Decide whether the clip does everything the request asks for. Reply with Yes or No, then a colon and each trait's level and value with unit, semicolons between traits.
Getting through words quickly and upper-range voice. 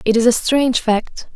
Yes: fast, 220 wpm; high, 235 Hz